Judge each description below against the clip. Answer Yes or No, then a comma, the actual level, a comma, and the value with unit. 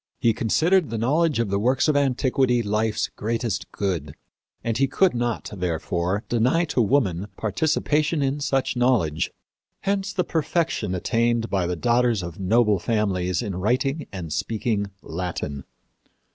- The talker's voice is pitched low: Yes, low, 115 Hz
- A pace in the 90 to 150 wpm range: Yes, average, 145 wpm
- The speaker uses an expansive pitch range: Yes, wide, 5.8 semitones